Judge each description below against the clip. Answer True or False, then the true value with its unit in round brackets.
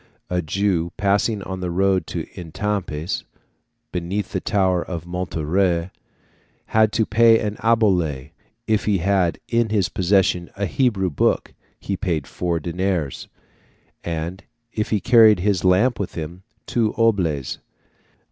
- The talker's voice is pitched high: False (95 Hz)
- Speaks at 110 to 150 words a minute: True (135 wpm)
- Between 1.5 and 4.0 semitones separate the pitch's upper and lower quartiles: True (3.4 semitones)